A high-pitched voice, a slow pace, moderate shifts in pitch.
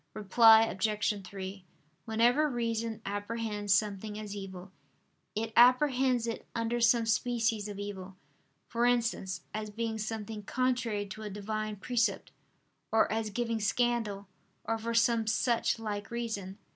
No: high, 220 Hz; slow, 130 wpm; narrow, 2.3 semitones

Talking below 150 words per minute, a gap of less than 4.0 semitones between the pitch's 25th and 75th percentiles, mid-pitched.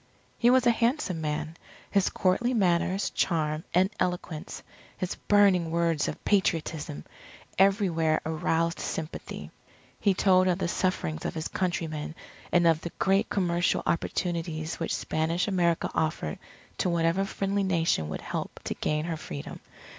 Yes: average, 140 wpm; average, 3.1 semitones; medium, 170 Hz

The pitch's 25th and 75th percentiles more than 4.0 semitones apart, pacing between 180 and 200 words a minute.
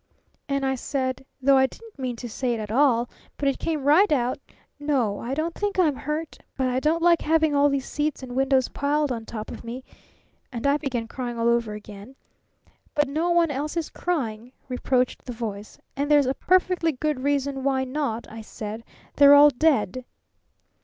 No: average, 3.6 semitones; average, 195 wpm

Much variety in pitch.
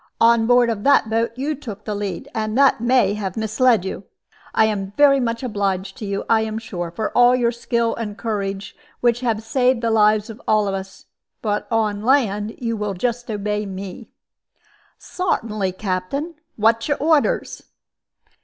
No: average, 2.8 semitones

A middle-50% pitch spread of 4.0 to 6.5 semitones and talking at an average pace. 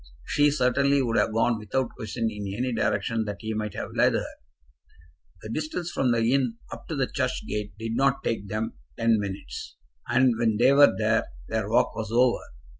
No: average, 3.0 semitones; average, 190 wpm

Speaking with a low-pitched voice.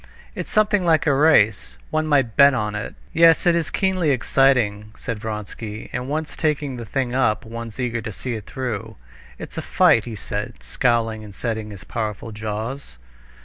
Yes: low, 120 Hz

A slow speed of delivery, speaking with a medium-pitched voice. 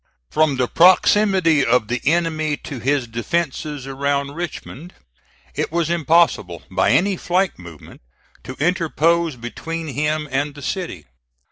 Yes: slow, 130 wpm; medium, 150 Hz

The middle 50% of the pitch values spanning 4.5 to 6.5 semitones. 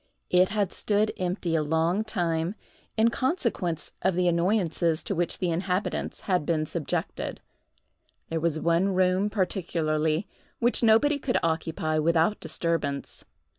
No: average, 3.6 semitones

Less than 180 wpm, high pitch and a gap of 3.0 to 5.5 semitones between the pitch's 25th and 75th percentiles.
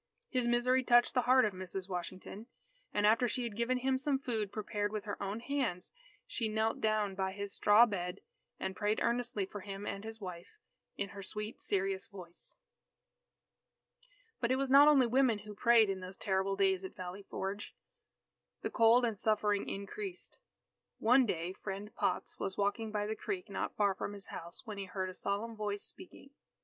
No: average, 185 wpm; high, 210 Hz; average, 3.6 semitones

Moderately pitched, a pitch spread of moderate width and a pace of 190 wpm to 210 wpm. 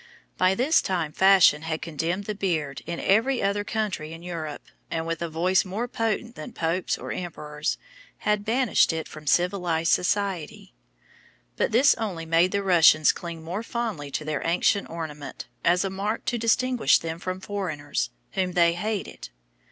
No: medium, 180 Hz; average, 4.0 semitones; average, 165 wpm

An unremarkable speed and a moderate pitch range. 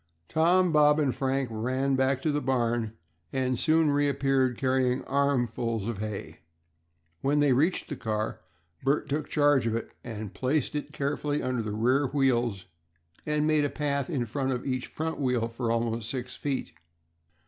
Yes: average, 160 wpm; average, 3.5 semitones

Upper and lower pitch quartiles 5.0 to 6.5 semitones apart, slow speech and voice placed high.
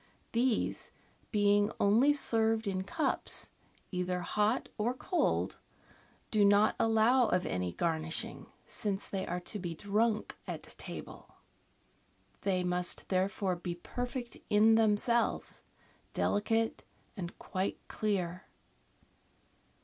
No: average, 3.6 semitones; slow, 105 wpm; high, 205 Hz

